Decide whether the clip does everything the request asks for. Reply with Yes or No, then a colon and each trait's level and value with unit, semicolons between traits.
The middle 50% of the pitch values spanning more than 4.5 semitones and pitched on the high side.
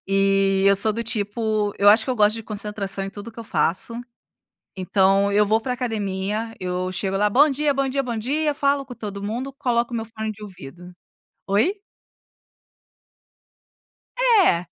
No: average, 3.3 semitones; high, 210 Hz